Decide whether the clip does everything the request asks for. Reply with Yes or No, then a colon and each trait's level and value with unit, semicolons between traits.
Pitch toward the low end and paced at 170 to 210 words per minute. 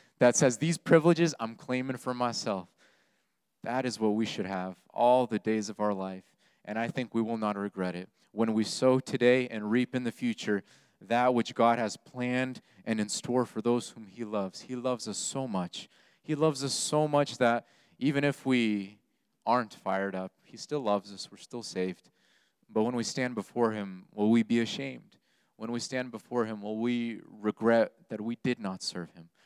Yes: low, 115 Hz; average, 200 wpm